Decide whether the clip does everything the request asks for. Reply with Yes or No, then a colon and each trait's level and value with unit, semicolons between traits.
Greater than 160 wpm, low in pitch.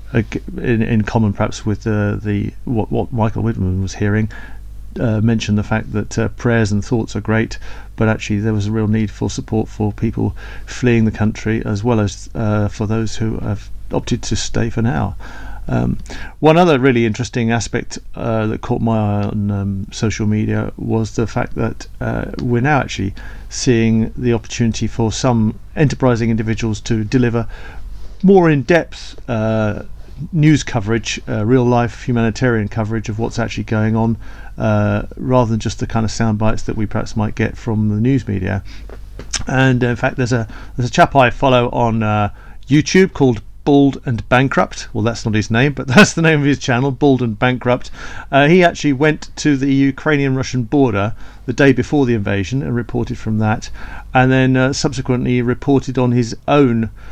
Yes: average, 180 wpm; low, 115 Hz